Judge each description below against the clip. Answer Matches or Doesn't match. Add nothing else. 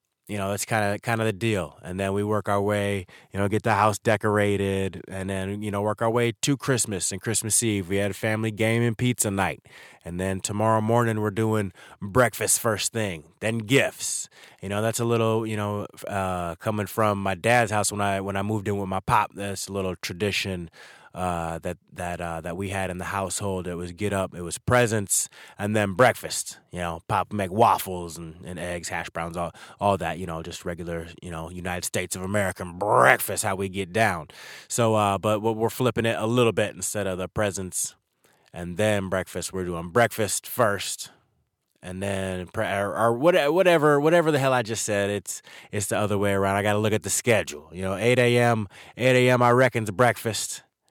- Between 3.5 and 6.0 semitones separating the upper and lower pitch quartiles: Doesn't match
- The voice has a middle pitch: Doesn't match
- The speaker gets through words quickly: Matches